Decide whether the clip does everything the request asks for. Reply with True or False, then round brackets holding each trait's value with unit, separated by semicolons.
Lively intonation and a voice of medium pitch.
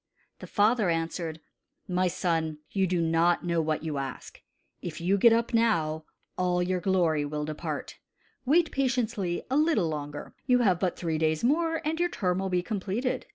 True (5.9 semitones; 180 Hz)